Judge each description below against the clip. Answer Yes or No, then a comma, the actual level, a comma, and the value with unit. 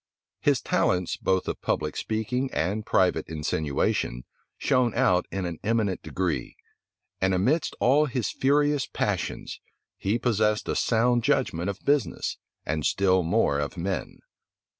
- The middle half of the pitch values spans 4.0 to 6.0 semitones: Yes, wide, 5.5 semitones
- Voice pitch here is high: No, low, 100 Hz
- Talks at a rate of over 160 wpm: No, slow, 135 wpm